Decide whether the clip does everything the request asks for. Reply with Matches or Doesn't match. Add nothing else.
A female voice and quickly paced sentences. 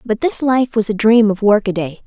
Matches